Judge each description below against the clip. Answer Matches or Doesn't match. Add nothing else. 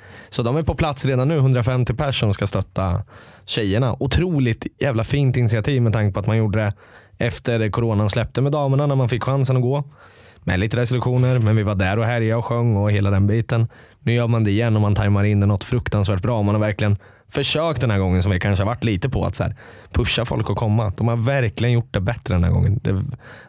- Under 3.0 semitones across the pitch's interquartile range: Doesn't match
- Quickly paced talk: Matches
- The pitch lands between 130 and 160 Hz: Doesn't match